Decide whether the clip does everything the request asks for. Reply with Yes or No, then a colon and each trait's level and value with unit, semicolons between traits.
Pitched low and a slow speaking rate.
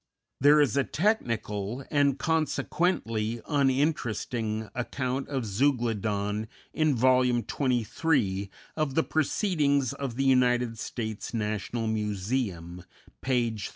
Yes: low, 125 Hz; slow, 105 wpm